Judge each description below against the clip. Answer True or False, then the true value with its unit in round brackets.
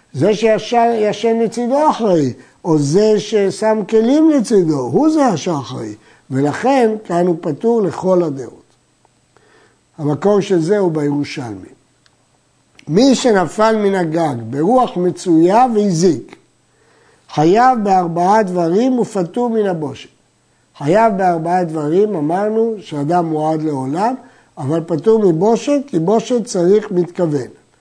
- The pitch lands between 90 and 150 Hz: False (185 Hz)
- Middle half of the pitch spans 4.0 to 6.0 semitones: True (5.5 semitones)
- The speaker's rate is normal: True (110 wpm)